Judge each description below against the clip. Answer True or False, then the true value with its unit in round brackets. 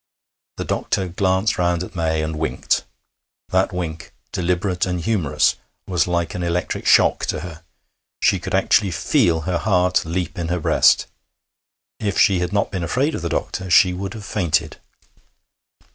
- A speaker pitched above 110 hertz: False (90 Hz)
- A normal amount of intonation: False (2.0 semitones)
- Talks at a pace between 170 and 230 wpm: False (160 wpm)